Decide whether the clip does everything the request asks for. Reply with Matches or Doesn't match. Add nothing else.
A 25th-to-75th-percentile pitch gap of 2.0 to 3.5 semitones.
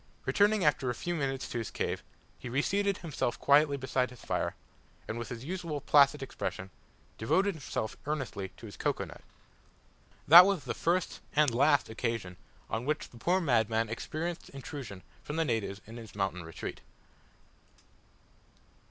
Doesn't match